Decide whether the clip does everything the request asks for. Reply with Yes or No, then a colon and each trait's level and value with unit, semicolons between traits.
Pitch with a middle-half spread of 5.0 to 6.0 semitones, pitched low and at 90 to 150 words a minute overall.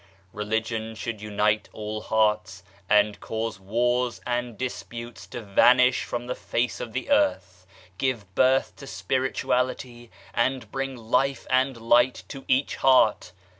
No: average, 2.9 semitones; low, 120 Hz; slow, 135 wpm